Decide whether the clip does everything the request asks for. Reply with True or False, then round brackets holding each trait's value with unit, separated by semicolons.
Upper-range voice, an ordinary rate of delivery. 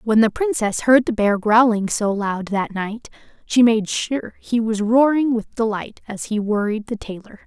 True (220 Hz; 195 wpm)